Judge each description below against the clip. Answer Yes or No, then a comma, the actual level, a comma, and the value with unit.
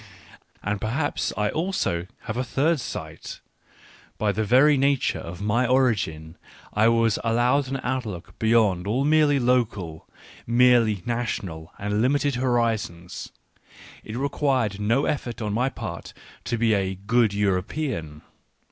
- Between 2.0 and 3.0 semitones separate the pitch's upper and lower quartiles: No, average, 4.2 semitones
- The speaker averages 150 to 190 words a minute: No, slow, 135 wpm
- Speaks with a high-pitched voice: No, low, 115 Hz